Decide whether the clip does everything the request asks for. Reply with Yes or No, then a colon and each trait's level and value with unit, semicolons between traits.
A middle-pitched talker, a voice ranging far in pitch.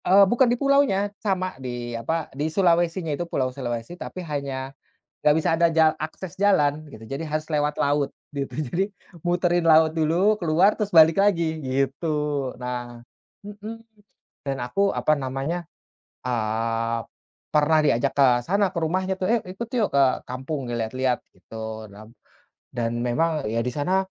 Yes: medium, 155 Hz; wide, 5.9 semitones